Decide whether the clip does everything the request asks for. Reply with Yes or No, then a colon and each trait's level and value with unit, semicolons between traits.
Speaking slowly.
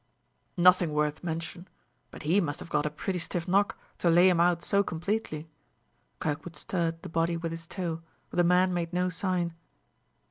No: average, 180 wpm